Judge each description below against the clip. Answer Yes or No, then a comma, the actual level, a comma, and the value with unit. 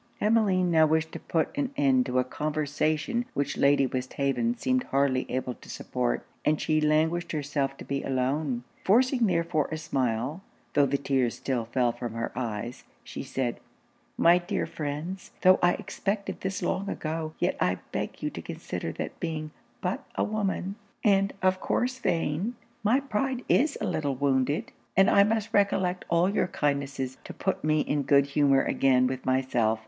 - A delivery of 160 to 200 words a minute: Yes, average, 170 wpm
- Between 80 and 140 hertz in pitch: No, medium, 155 Hz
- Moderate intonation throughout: No, wide, 6.2 semitones